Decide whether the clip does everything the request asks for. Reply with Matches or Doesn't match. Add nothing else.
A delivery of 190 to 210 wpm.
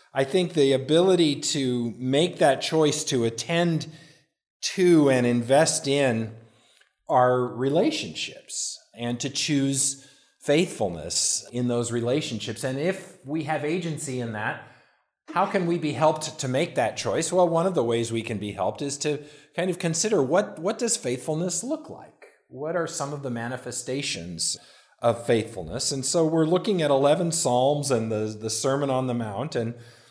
Doesn't match